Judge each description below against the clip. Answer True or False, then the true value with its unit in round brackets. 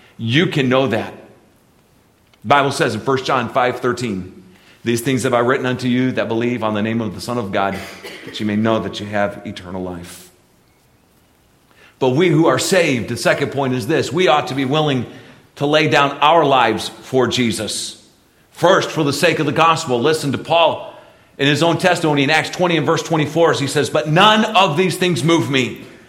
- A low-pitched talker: True (130 Hz)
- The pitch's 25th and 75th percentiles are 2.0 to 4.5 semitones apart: False (5.5 semitones)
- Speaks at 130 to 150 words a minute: False (205 wpm)